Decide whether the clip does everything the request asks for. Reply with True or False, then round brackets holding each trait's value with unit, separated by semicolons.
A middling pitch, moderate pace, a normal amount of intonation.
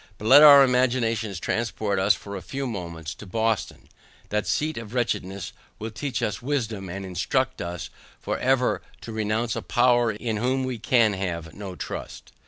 False (110 Hz; 175 wpm; 4.1 semitones)